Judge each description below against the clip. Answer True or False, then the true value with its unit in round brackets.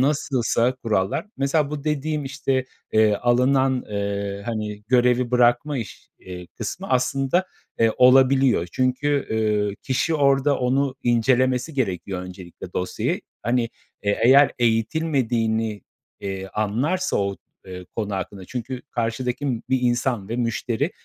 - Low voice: True (125 Hz)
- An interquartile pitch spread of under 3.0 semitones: False (4.1 semitones)